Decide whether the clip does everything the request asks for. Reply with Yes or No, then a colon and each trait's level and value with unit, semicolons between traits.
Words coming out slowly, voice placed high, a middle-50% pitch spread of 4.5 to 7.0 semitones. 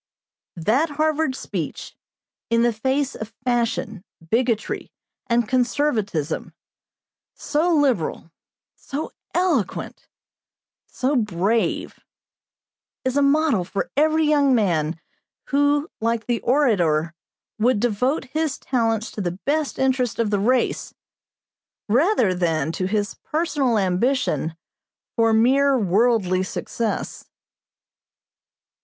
Yes: slow, 105 wpm; high, 235 Hz; wide, 5.5 semitones